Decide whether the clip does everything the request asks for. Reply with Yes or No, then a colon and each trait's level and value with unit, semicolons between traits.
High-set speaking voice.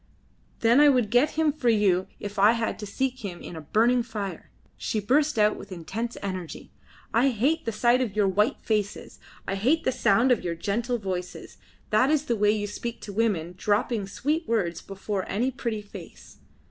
Yes: high, 215 Hz